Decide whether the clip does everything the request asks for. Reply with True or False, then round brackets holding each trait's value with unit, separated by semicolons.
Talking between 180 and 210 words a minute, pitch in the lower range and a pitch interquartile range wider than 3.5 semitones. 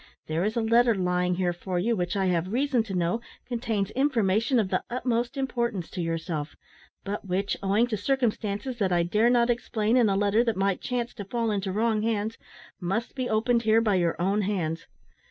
False (200 wpm; 210 Hz; 4.1 semitones)